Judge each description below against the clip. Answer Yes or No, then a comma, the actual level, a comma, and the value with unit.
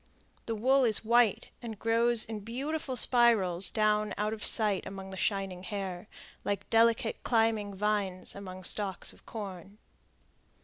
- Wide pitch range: No, average, 2.8 semitones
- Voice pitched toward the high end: Yes, high, 210 Hz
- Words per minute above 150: No, average, 140 wpm